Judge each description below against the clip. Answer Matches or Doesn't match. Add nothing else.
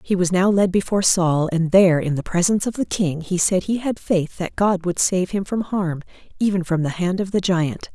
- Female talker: Matches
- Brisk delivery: Matches